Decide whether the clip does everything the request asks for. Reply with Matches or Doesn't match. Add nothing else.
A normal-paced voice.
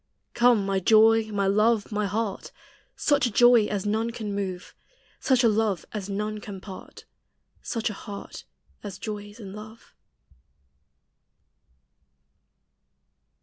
Doesn't match